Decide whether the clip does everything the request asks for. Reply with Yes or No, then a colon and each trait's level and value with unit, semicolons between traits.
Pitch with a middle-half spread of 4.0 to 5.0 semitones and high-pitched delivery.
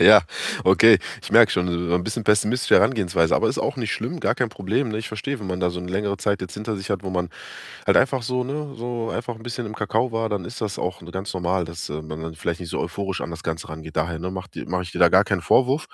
No: average, 4.3 semitones; very low, 95 Hz